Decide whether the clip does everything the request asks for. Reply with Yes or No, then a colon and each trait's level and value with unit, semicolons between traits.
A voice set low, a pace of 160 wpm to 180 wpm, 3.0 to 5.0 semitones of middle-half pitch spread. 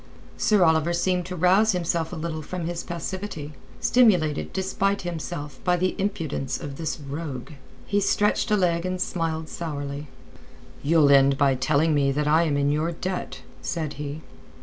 No: medium, 165 Hz; average, 165 wpm; average, 3.6 semitones